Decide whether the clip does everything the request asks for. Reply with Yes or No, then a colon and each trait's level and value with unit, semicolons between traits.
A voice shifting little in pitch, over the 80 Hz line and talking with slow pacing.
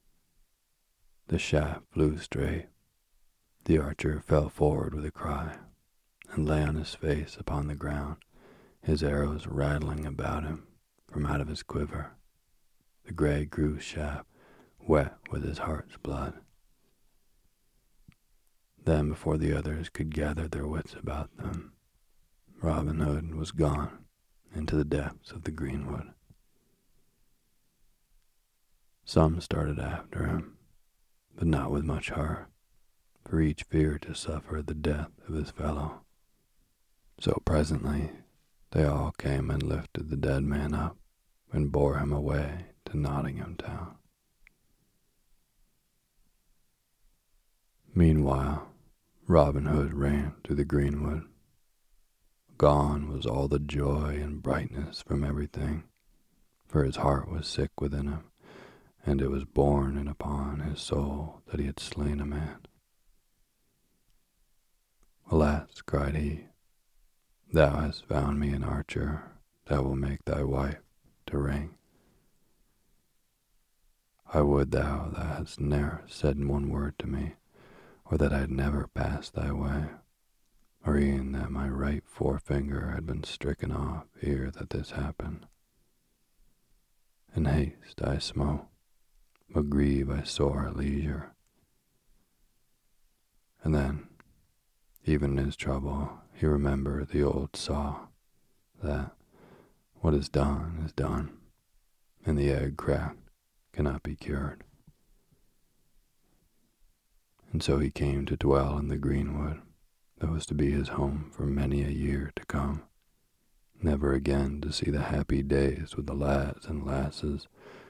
No: narrow, 1.4 semitones; very low, 75 Hz; slow, 125 wpm